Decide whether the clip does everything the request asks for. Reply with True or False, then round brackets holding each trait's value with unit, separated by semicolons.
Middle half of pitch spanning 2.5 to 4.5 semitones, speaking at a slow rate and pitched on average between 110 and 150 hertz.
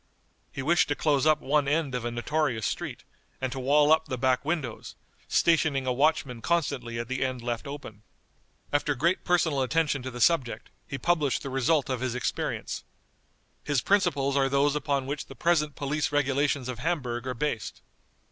False (3.0 semitones; 180 wpm; 140 Hz)